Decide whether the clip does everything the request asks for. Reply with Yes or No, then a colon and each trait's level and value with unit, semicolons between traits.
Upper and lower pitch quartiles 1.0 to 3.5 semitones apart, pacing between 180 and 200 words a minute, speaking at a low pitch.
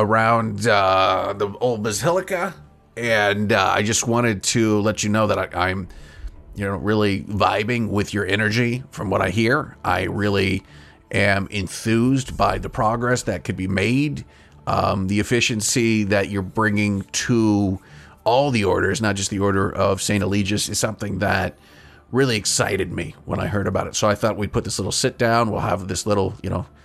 Yes: average, 3.0 semitones; average, 185 wpm; low, 105 Hz